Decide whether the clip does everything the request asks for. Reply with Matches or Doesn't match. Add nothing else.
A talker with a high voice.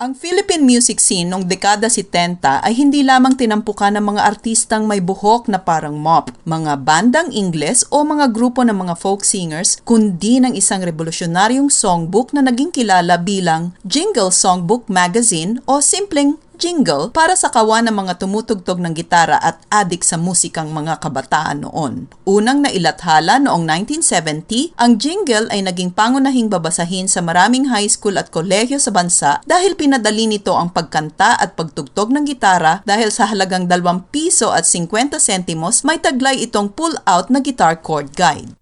Matches